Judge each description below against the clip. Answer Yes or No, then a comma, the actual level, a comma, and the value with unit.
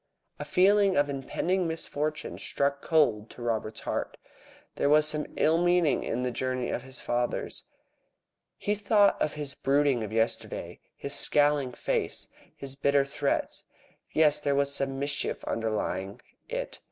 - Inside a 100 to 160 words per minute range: Yes, average, 145 wpm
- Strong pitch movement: No, average, 3.3 semitones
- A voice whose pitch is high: No, medium, 140 Hz